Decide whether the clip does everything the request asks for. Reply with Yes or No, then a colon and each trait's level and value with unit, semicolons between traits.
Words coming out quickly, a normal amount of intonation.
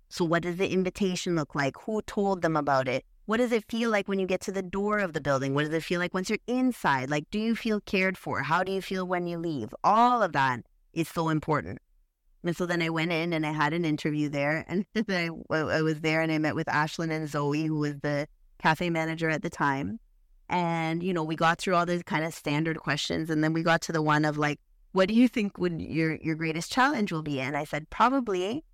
Yes: fast, 250 wpm; average, 3.9 semitones